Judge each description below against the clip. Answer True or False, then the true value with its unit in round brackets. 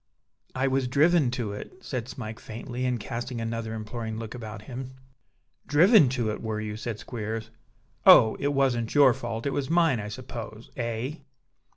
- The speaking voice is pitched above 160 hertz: False (120 Hz)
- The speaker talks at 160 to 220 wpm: True (170 wpm)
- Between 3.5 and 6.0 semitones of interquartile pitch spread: False (3.1 semitones)